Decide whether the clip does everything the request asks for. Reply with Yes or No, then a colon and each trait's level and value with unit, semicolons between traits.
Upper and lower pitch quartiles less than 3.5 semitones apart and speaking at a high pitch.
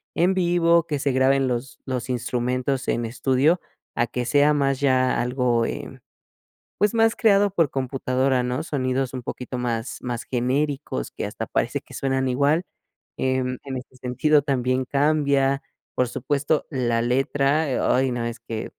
No: narrow, 2.4 semitones; low, 130 Hz